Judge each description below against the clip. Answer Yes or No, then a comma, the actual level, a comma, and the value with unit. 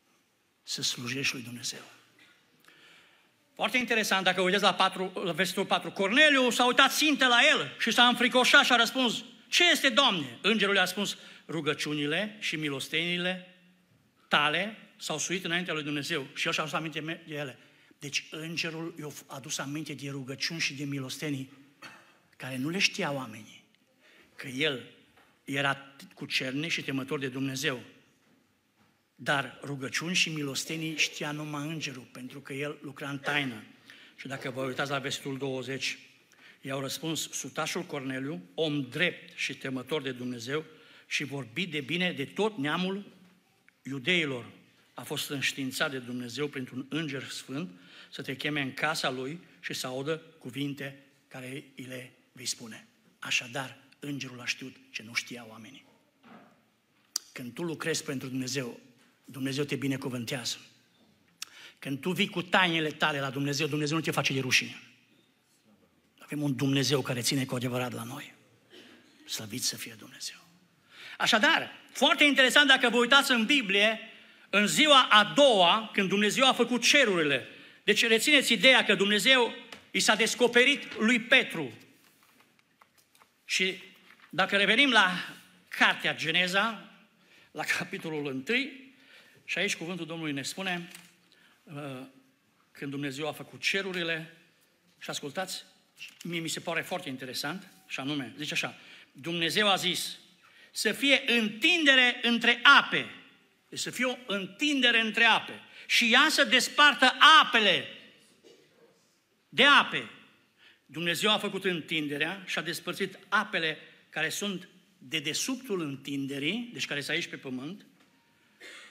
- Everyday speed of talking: Yes, average, 140 wpm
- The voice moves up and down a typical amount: No, wide, 6.4 semitones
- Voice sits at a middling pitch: Yes, medium, 160 Hz